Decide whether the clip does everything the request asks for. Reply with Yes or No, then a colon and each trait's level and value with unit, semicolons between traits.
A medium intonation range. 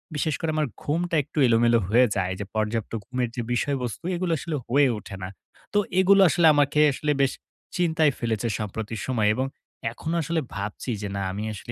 No: wide, 6.0 semitones